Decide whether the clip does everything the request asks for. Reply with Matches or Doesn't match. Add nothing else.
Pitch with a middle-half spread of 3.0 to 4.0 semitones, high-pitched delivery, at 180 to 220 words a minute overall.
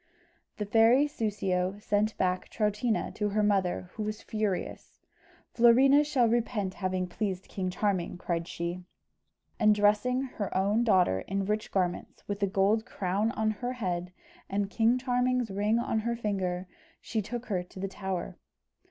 Doesn't match